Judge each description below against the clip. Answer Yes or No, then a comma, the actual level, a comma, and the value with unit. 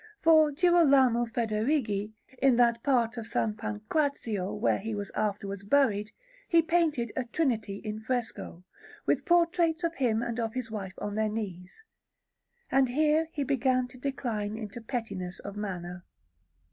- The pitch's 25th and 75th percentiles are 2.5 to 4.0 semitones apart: No, average, 4.9 semitones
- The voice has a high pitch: Yes, high, 235 Hz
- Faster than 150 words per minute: No, average, 145 wpm